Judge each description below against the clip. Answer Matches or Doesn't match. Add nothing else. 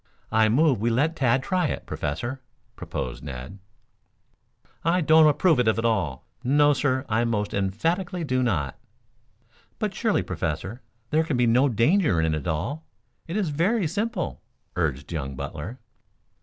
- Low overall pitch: Matches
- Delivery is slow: Doesn't match